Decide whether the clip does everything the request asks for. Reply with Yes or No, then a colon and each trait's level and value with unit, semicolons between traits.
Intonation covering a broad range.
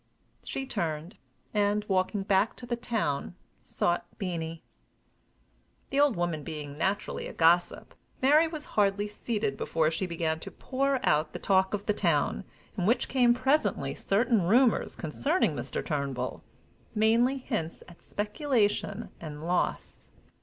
Yes: wide, 6.3 semitones